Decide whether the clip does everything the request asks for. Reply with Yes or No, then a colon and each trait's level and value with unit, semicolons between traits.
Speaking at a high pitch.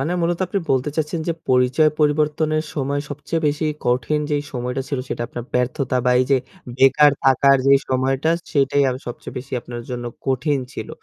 No: medium, 140 Hz